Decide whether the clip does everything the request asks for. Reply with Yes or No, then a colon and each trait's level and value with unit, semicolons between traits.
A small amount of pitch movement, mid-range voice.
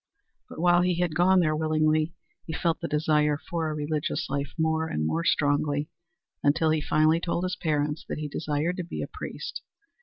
Yes: narrow, 1.9 semitones; medium, 155 Hz